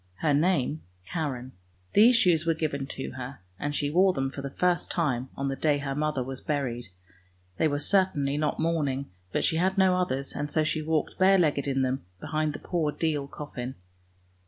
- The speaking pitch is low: No, medium, 150 Hz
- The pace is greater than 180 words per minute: Yes, average, 195 wpm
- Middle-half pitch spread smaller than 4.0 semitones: Yes, average, 3.1 semitones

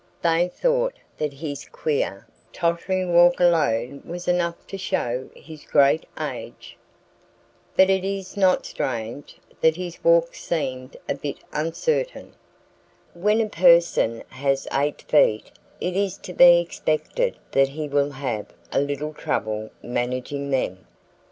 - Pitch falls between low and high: Yes, medium, 160 Hz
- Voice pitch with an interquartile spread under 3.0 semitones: No, average, 4.8 semitones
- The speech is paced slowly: Yes, slow, 130 wpm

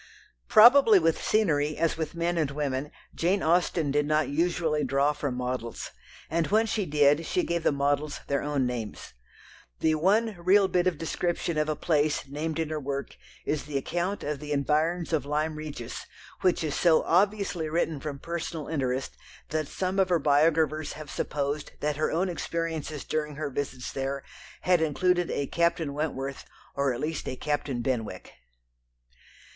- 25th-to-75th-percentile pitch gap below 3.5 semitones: Yes, average, 3.1 semitones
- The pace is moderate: Yes, average, 170 wpm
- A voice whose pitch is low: No, medium, 155 Hz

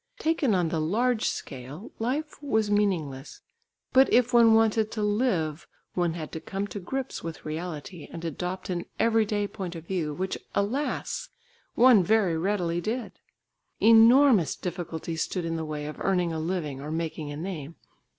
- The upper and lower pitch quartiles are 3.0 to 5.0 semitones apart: No, wide, 5.5 semitones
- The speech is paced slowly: No, average, 160 wpm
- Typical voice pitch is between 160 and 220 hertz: Yes, medium, 185 Hz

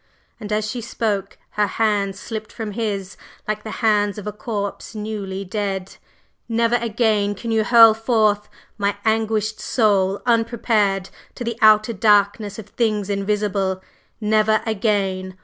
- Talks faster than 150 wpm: No, average, 140 wpm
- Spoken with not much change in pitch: Yes, narrow, 1.7 semitones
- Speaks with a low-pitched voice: No, high, 210 Hz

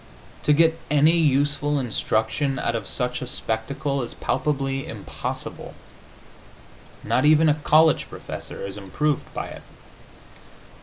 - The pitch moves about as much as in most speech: Yes, average, 3.3 semitones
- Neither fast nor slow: No, slow, 120 wpm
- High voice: No, medium, 140 Hz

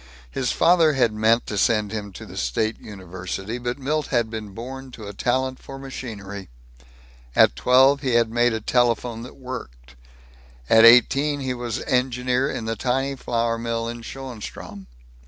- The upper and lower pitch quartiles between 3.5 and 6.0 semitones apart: No, average, 3.1 semitones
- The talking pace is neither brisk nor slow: Yes, average, 165 wpm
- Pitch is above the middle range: No, low, 120 Hz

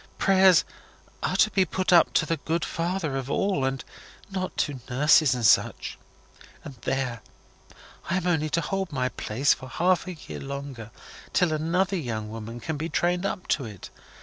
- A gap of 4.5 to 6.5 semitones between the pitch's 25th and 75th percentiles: Yes, wide, 5.5 semitones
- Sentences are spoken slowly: No, average, 175 wpm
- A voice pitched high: No, medium, 155 Hz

